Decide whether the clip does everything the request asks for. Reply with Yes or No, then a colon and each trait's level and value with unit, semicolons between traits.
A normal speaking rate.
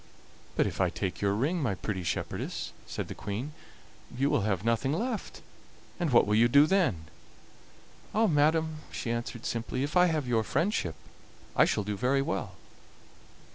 Yes: average, 170 wpm